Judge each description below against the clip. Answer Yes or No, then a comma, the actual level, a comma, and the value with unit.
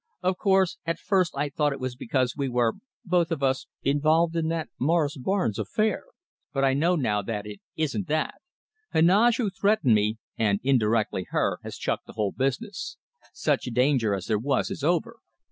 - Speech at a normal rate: Yes, average, 180 wpm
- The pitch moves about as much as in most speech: No, wide, 6.1 semitones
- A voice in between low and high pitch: Yes, medium, 145 Hz